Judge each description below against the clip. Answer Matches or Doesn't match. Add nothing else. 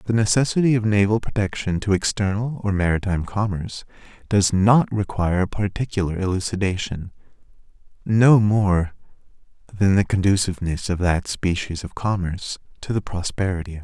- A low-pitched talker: Matches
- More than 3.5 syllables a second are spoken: Matches